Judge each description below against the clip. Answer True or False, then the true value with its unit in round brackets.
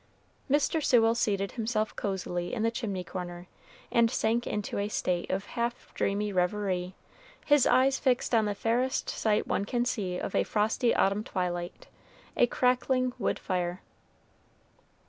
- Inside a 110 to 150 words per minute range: True (145 wpm)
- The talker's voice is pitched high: True (210 Hz)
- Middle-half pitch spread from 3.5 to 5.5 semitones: True (4.3 semitones)